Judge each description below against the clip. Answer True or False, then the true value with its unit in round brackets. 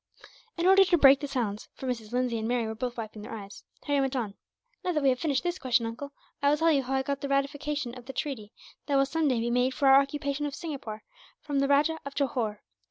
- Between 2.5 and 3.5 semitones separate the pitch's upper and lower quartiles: True (3.2 semitones)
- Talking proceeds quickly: True (255 wpm)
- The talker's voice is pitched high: True (270 Hz)